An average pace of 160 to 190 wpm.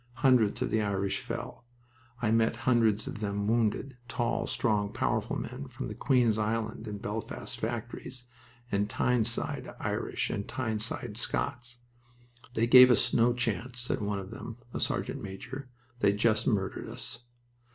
No: average, 145 wpm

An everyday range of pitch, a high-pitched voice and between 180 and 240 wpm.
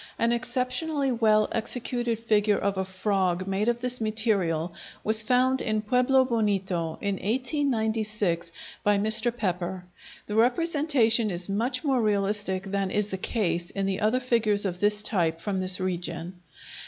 No: average, 4.0 semitones; high, 210 Hz; average, 150 wpm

